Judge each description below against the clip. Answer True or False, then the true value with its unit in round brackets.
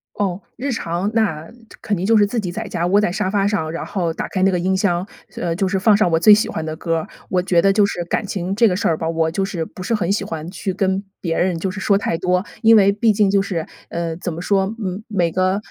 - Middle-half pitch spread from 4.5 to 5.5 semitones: False (2.9 semitones)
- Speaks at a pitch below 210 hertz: True (190 Hz)